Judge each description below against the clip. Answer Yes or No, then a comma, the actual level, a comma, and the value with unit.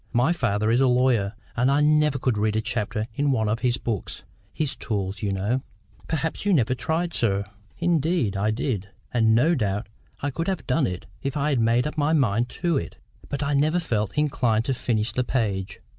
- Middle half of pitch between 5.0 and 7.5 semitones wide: Yes, average, 5.3 semitones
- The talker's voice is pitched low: Yes, low, 125 Hz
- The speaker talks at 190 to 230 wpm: Yes, fast, 205 wpm